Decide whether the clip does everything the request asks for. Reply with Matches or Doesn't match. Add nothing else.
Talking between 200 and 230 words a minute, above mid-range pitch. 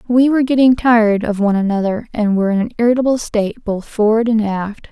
Matches